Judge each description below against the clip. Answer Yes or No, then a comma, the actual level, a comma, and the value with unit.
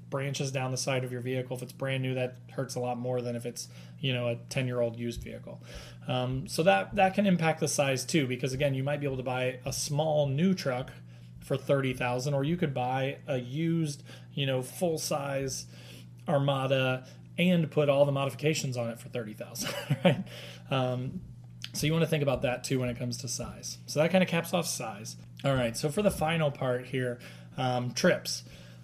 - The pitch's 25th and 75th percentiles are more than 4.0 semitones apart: No, average, 3.3 semitones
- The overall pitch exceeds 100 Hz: Yes, low, 130 Hz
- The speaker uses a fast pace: Yes, fast, 210 wpm